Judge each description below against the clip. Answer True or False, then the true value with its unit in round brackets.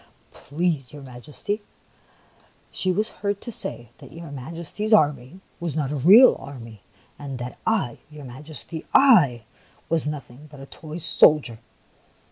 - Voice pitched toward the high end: False (150 Hz)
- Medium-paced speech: True (145 wpm)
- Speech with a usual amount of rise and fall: True (4.5 semitones)